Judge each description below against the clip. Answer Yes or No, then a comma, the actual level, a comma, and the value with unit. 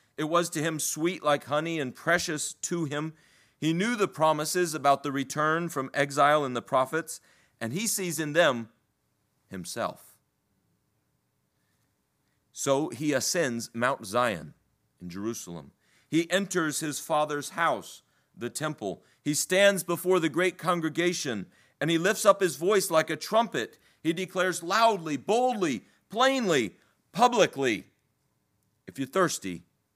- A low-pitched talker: No, medium, 155 Hz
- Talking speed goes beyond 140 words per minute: No, slow, 135 wpm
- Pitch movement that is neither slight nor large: Yes, average, 4.3 semitones